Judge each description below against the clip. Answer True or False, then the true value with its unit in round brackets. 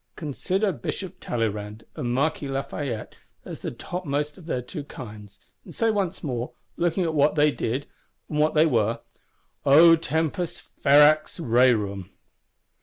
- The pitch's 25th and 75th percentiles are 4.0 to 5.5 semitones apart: True (5.2 semitones)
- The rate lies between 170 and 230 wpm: False (140 wpm)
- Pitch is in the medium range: True (145 Hz)